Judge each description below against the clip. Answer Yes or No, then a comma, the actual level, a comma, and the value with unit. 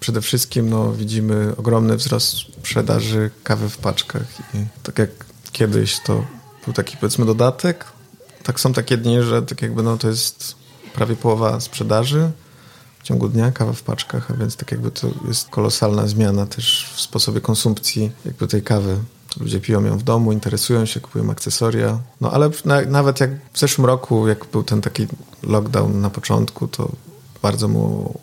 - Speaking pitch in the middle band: No, low, 115 Hz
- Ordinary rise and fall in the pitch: Yes, average, 3.2 semitones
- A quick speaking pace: Yes, fast, 170 wpm